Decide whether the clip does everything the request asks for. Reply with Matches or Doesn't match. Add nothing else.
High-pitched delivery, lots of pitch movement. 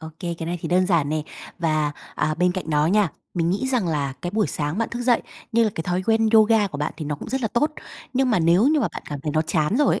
Doesn't match